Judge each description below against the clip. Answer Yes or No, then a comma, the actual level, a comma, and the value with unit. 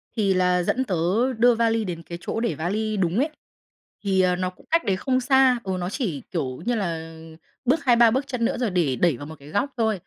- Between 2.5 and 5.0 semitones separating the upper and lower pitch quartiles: No, wide, 5.5 semitones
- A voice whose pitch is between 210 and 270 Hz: No, high, 200 Hz